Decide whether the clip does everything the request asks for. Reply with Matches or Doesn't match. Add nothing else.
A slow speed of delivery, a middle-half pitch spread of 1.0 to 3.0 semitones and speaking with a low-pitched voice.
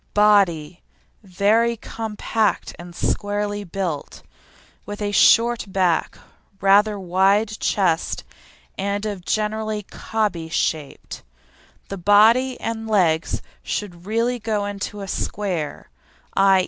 Doesn't match